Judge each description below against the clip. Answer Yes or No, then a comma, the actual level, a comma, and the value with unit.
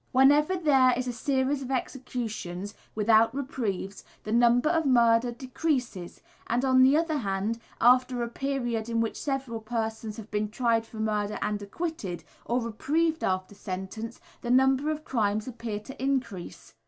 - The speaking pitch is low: No, high, 240 Hz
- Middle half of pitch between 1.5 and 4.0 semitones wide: Yes, average, 3.6 semitones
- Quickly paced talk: No, average, 155 wpm